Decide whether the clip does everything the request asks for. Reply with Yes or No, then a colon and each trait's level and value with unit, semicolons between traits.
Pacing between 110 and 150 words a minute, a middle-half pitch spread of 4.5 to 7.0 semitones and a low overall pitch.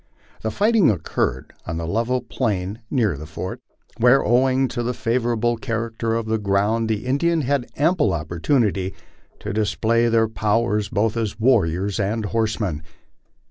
No: average, 145 wpm; average, 3.1 semitones; low, 115 Hz